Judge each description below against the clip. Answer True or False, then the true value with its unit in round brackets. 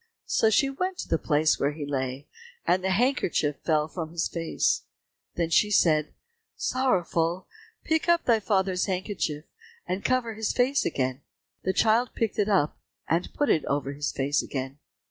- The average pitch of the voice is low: False (180 Hz)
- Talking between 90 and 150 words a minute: False (165 wpm)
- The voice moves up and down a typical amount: False (6.8 semitones)